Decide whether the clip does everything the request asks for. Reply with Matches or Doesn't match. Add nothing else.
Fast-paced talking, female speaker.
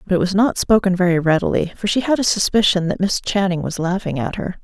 Matches